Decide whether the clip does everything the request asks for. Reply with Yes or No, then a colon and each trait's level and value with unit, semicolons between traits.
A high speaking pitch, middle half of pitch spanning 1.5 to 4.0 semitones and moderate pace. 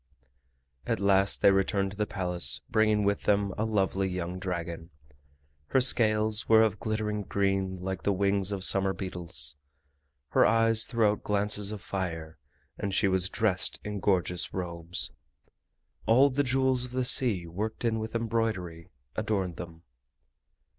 No: low, 100 Hz; average, 3.0 semitones; average, 150 wpm